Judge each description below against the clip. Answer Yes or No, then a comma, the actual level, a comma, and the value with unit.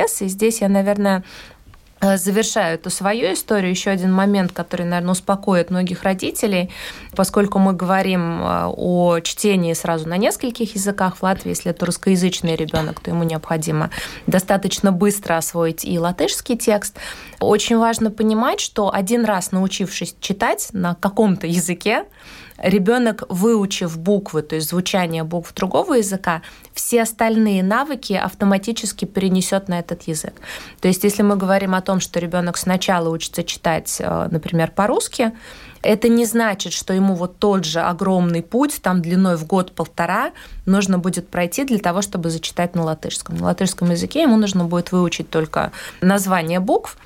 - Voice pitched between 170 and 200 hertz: Yes, high, 190 Hz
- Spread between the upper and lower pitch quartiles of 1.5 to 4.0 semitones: Yes, average, 2.9 semitones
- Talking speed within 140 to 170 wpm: Yes, average, 145 wpm